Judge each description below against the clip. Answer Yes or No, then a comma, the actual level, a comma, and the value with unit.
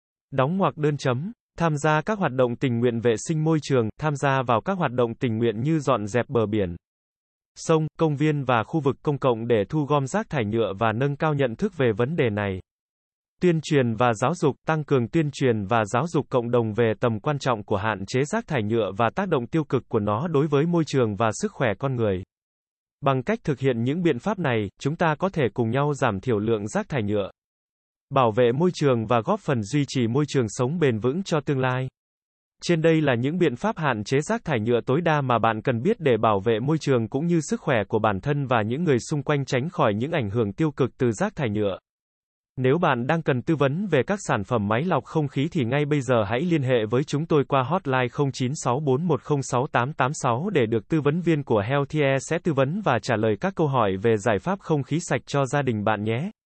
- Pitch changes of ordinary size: Yes, average, 4.7 semitones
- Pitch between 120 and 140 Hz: Yes, low, 135 Hz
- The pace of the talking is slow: No, average, 240 wpm